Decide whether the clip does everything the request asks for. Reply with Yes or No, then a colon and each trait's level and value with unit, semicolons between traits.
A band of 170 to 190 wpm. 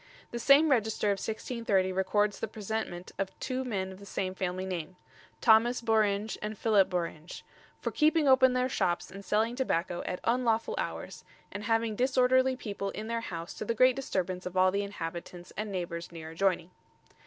Yes: average, 175 wpm